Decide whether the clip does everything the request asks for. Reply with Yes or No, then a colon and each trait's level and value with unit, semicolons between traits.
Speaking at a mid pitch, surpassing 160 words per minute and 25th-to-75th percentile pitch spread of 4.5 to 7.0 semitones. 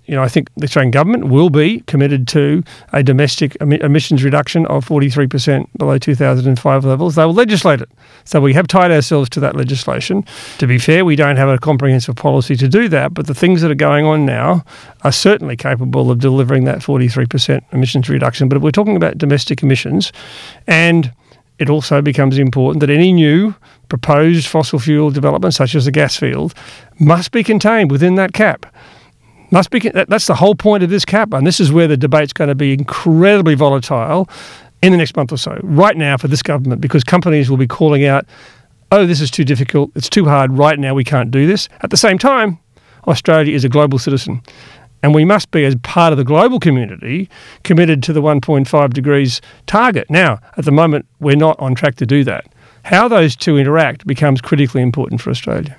No: medium, 145 Hz; average, 200 wpm; average, 3.4 semitones